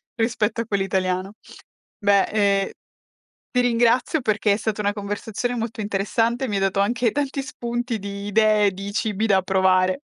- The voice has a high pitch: Yes, high, 210 Hz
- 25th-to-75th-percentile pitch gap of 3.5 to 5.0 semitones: No, average, 2.9 semitones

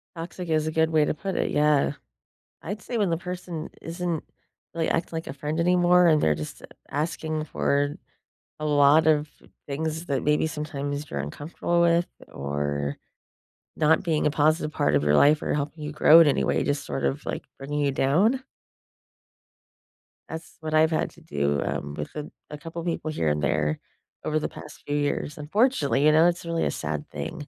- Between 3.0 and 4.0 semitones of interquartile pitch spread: No, narrow, 2.6 semitones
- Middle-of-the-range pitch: Yes, medium, 150 Hz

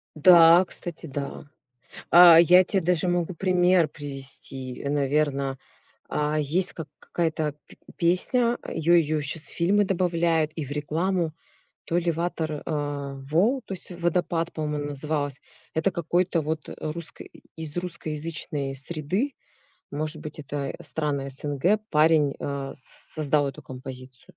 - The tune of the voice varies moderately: Yes, average, 3.1 semitones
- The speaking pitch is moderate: Yes, medium, 155 Hz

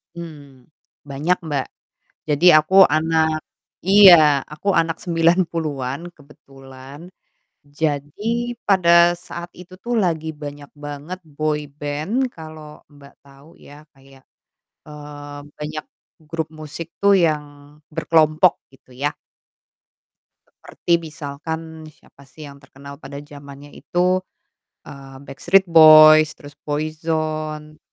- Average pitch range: No, narrow, 2.2 semitones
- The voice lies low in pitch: No, medium, 155 Hz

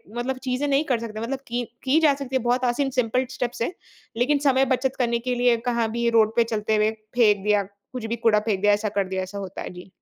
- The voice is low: No, high, 235 Hz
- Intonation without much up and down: No, average, 3.3 semitones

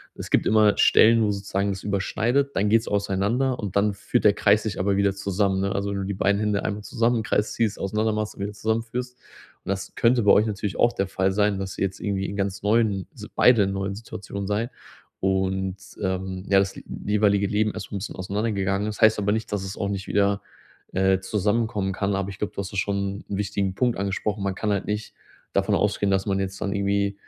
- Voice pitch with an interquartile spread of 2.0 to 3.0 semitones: No, narrow, 1.6 semitones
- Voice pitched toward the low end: Yes, low, 100 Hz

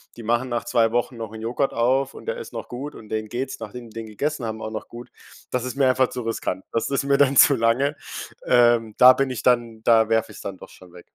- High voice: No, low, 120 Hz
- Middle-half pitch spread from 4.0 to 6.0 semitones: No, average, 2.7 semitones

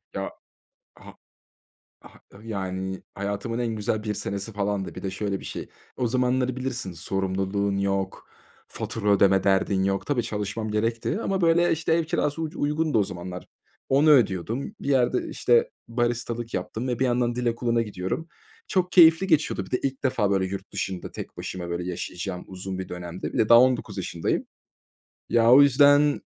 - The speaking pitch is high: No, low, 110 Hz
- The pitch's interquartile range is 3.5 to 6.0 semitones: Yes, average, 5.1 semitones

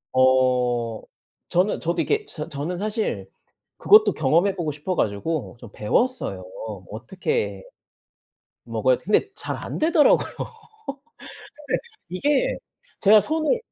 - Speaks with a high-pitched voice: No, medium, 180 Hz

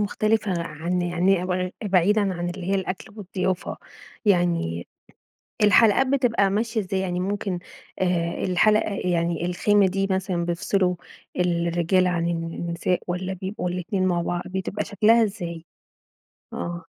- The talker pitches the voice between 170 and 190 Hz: Yes, medium, 185 Hz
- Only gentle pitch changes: Yes, narrow, 2.3 semitones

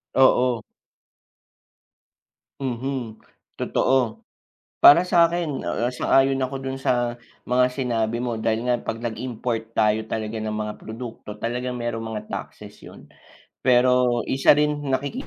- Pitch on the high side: No, low, 120 Hz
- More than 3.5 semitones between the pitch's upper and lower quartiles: No, average, 2.8 semitones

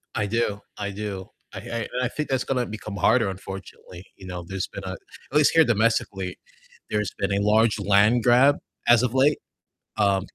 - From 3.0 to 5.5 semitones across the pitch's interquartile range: Yes, average, 3.5 semitones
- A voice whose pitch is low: Yes, low, 105 Hz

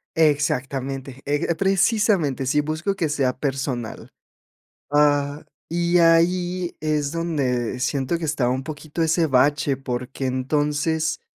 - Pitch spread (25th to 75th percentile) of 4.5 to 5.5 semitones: No, average, 3.7 semitones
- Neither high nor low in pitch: Yes, medium, 145 Hz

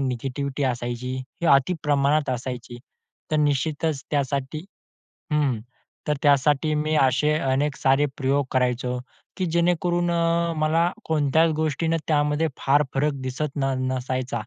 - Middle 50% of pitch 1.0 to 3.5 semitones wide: Yes, average, 3.0 semitones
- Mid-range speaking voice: Yes, medium, 145 Hz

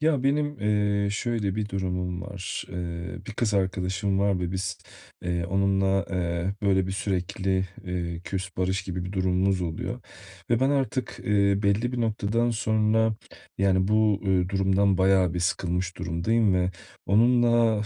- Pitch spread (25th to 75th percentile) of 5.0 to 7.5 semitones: No, average, 2.7 semitones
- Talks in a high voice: No, very low, 95 Hz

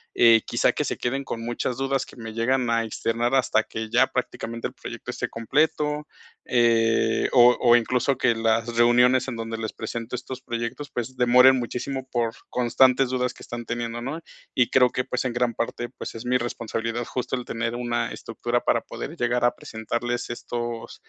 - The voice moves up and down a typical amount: No, narrow, 1.6 semitones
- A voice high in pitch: No, low, 120 Hz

